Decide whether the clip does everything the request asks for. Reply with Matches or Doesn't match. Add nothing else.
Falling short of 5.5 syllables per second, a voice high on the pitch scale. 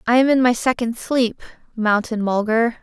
Matches